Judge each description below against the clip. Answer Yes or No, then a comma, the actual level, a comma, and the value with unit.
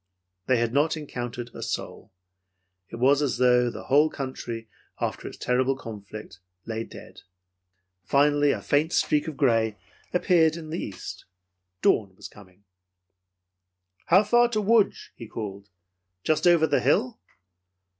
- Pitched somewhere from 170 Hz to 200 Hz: No, low, 135 Hz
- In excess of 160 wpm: No, average, 140 wpm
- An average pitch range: No, wide, 5.8 semitones